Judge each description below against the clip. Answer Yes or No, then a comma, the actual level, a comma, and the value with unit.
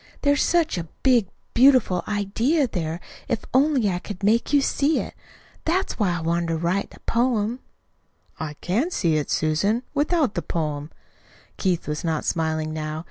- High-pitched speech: Yes, high, 200 Hz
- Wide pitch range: Yes, wide, 8.0 semitones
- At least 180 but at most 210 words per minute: No, average, 165 wpm